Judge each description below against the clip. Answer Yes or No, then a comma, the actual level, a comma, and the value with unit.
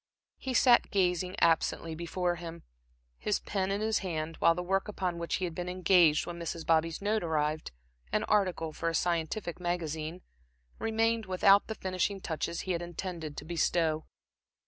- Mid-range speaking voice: Yes, medium, 175 Hz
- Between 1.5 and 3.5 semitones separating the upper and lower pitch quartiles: Yes, average, 2.8 semitones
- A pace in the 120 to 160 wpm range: No, average, 170 wpm